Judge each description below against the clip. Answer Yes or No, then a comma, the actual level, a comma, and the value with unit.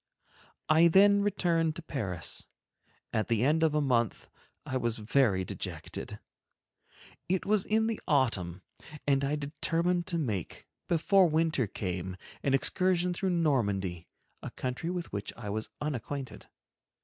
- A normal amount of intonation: No, wide, 7.4 semitones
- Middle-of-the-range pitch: Yes, medium, 145 Hz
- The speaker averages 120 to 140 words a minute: Yes, slow, 135 wpm